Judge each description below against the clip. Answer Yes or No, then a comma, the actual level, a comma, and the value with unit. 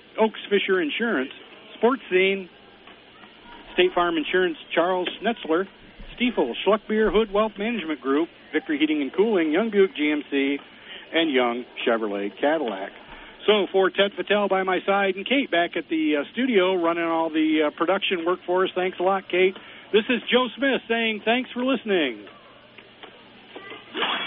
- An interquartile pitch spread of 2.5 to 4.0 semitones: No, average, 4.7 semitones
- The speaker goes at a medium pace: Yes, average, 150 wpm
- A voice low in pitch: No, high, 190 Hz